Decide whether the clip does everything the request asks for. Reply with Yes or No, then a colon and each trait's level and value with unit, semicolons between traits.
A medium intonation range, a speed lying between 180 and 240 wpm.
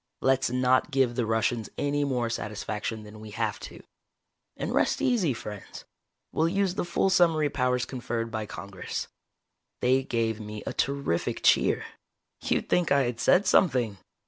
No: average, 4.4 semitones; average, 155 wpm